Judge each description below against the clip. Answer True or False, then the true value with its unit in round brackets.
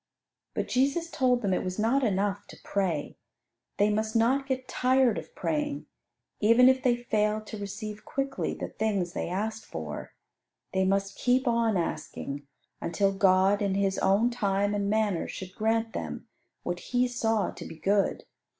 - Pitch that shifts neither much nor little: True (3.9 semitones)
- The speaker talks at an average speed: True (165 wpm)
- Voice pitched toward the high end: True (215 Hz)